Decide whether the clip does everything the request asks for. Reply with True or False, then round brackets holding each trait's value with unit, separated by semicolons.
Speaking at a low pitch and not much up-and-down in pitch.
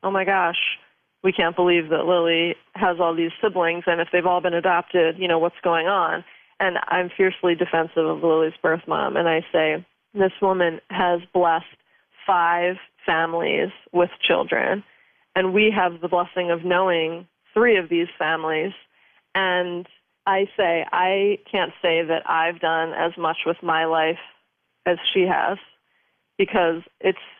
False (175 Hz; 1.8 semitones)